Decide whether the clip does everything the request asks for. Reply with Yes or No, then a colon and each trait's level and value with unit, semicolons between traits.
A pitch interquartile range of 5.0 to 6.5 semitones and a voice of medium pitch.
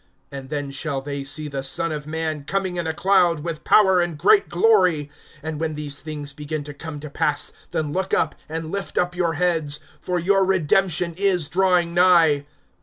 No: average, 3.3 semitones; medium, 160 Hz